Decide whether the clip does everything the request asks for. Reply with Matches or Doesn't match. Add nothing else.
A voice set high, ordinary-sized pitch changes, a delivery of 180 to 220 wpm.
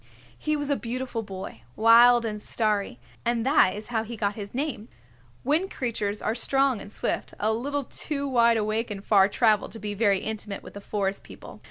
Matches